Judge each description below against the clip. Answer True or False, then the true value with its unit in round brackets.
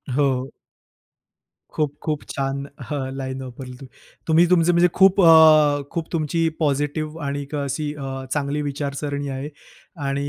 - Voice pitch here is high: False (145 Hz)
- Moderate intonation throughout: False (2.1 semitones)